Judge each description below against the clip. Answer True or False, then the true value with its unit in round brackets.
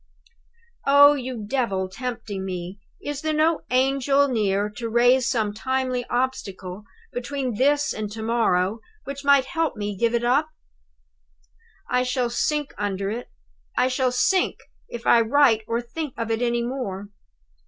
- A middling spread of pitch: True (4.1 semitones)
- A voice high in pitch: True (245 Hz)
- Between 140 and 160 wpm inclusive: True (155 wpm)